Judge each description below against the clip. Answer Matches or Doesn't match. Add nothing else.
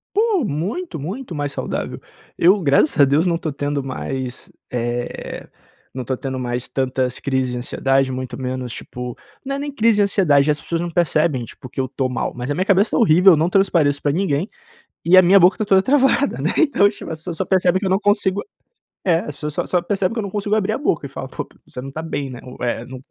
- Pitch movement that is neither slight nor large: Doesn't match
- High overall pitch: Doesn't match